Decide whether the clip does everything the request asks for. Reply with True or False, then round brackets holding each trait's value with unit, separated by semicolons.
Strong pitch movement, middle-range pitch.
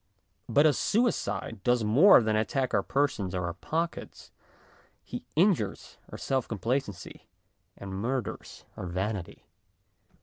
False (6.2 semitones; 115 Hz)